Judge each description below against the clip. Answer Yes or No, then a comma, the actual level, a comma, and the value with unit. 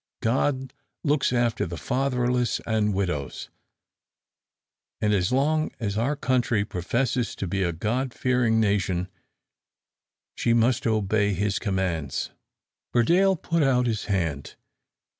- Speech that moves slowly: Yes, slow, 120 wpm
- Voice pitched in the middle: No, low, 110 Hz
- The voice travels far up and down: No, average, 4.5 semitones